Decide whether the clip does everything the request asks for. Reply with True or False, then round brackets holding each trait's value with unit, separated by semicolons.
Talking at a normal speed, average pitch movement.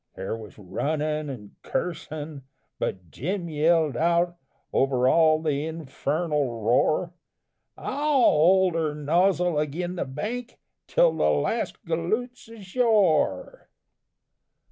False (105 wpm; 3.9 semitones)